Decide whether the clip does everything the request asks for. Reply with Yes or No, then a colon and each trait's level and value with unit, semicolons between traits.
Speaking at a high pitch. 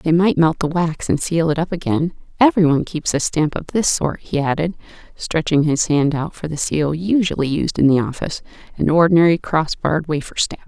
No: medium, 160 Hz